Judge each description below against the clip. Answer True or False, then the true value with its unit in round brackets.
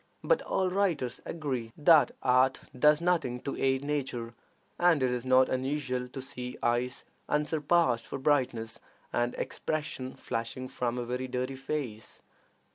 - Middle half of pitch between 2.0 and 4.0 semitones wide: True (3.2 semitones)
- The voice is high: False (130 Hz)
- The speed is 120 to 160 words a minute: True (140 wpm)